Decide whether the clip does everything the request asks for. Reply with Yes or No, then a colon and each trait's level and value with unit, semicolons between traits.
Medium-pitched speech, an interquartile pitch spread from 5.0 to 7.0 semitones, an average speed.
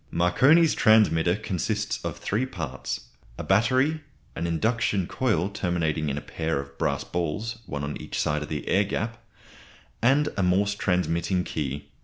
No: very low, 90 Hz; wide, 5.4 semitones; average, 155 wpm